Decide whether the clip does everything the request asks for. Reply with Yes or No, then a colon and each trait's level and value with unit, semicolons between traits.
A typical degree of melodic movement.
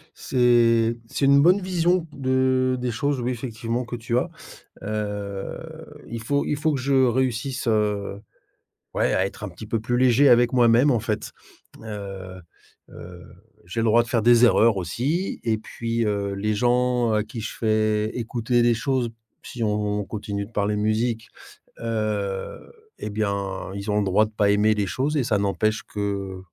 Yes: average, 3.2 semitones